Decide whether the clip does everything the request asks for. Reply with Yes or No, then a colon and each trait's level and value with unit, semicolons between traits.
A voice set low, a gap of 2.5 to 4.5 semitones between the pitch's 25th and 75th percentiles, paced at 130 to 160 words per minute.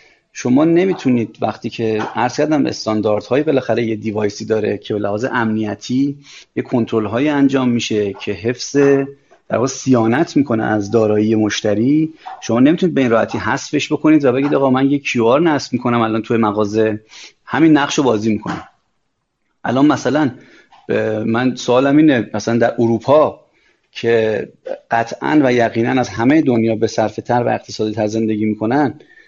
Yes: low, 115 Hz; average, 3.5 semitones; average, 150 wpm